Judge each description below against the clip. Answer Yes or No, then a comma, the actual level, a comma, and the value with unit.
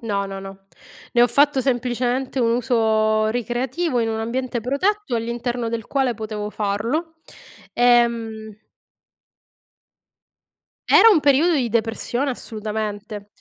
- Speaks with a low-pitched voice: No, high, 235 Hz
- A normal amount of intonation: Yes, average, 3.0 semitones